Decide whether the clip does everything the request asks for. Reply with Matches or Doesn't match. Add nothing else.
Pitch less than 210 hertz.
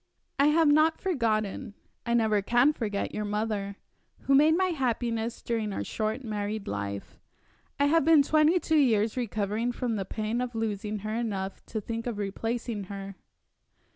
Doesn't match